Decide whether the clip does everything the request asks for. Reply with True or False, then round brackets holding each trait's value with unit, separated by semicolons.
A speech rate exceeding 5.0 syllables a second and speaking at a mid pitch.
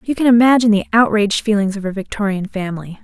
False (7.0 syllables/s; 210 Hz)